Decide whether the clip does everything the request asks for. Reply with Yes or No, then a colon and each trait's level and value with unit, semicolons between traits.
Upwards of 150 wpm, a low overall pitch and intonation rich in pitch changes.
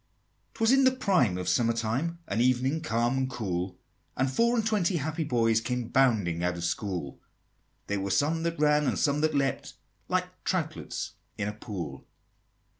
Yes: average, 175 wpm; low, 125 Hz; wide, 7.4 semitones